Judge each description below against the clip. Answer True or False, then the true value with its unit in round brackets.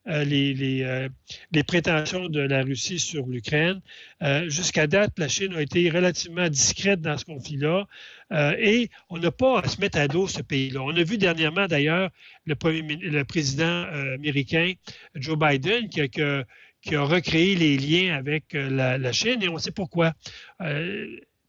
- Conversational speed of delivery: True (175 wpm)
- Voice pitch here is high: False (155 Hz)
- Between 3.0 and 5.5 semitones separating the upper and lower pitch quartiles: True (3.9 semitones)